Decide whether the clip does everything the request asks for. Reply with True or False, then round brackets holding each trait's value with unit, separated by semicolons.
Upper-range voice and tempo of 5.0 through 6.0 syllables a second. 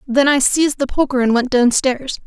True (265 Hz; 5.3 syllables/s)